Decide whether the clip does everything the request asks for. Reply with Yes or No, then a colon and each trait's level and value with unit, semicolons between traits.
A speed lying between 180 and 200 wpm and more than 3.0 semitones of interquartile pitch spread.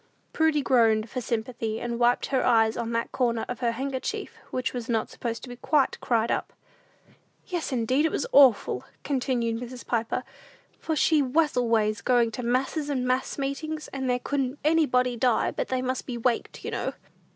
No: average, 185 wpm; narrow, 2.6 semitones